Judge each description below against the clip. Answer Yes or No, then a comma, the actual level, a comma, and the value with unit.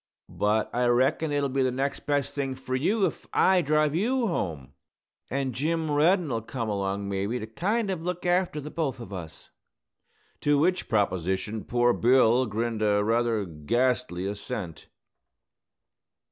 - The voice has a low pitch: Yes, low, 125 Hz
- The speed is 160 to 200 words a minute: No, average, 150 wpm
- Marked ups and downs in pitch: Yes, wide, 6.1 semitones